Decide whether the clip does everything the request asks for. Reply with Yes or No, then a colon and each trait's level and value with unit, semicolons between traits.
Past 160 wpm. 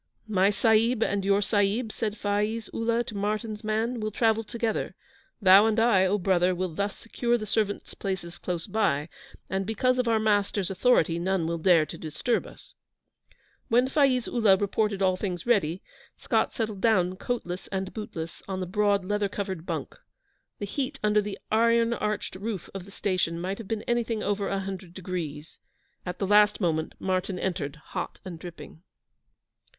Yes: average, 170 wpm